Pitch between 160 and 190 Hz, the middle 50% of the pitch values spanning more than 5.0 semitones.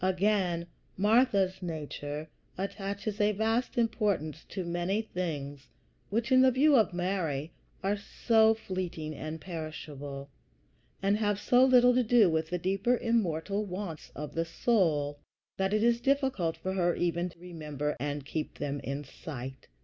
Yes: medium, 185 Hz; wide, 5.5 semitones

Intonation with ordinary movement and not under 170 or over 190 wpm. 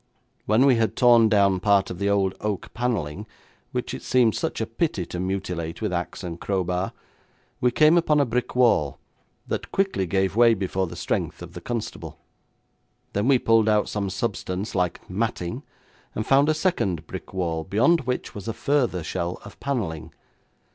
Yes: average, 4.8 semitones; average, 175 wpm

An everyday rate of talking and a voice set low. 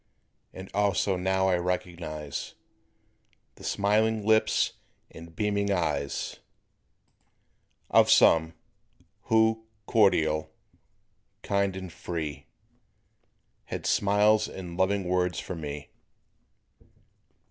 No: slow, 85 wpm; very low, 95 Hz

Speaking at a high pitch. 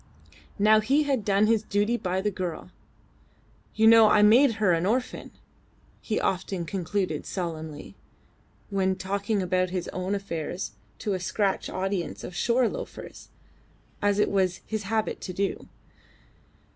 Yes: high, 200 Hz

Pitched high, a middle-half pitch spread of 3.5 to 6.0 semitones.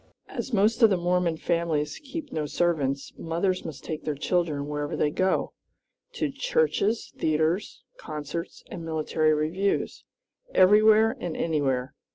No: medium, 170 Hz; average, 4.6 semitones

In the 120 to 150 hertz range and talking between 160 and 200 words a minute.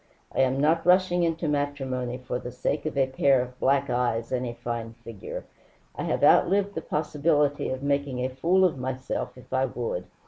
Yes: low, 135 Hz; average, 195 wpm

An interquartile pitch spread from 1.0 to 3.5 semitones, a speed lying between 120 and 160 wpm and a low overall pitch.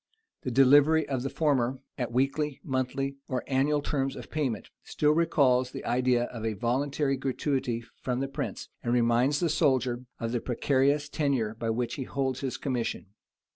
No: narrow, 2.5 semitones; average, 175 wpm; low, 130 Hz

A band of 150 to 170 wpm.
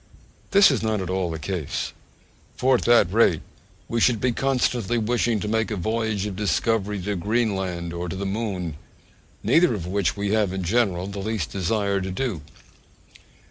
No: average, 180 wpm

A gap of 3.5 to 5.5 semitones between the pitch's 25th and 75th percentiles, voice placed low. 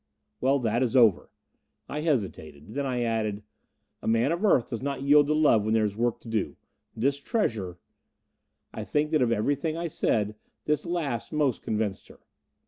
Yes: average, 5.1 semitones; low, 125 Hz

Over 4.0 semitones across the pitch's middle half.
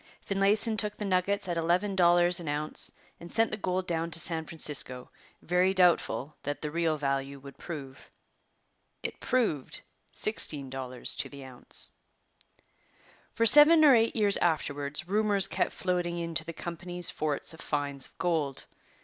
Yes: average, 4.8 semitones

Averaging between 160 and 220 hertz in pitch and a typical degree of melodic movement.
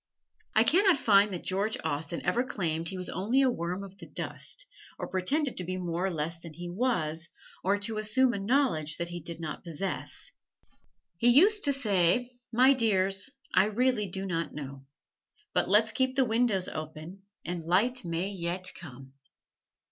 No: high, 190 Hz; wide, 5.9 semitones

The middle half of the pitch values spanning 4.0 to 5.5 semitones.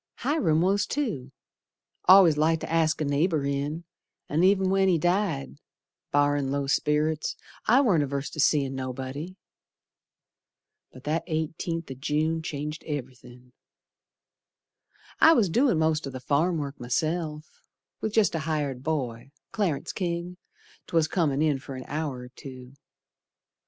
No: average, 3.6 semitones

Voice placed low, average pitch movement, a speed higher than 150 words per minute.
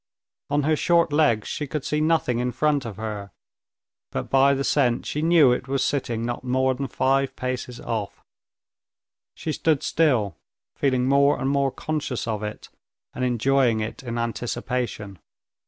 Yes: low, 130 Hz; average, 3.3 semitones; average, 160 wpm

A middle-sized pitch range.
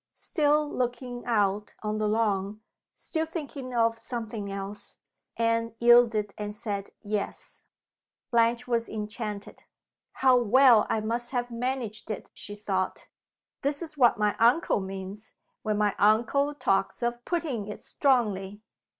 Yes: average, 3.0 semitones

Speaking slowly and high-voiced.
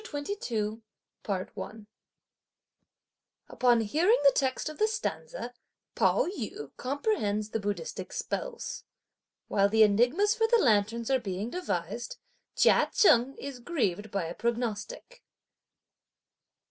Yes: slow, 110 wpm; high, 240 Hz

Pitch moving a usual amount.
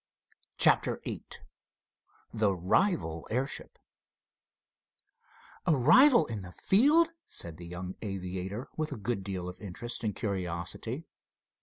No: wide, 7.4 semitones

